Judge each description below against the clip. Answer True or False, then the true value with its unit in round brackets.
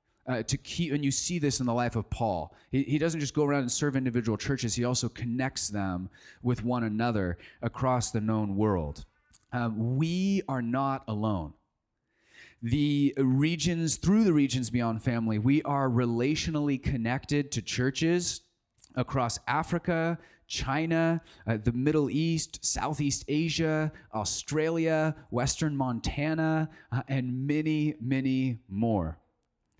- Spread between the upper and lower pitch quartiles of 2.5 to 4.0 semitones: False (4.6 semitones)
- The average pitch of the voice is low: True (130 Hz)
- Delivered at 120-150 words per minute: True (135 wpm)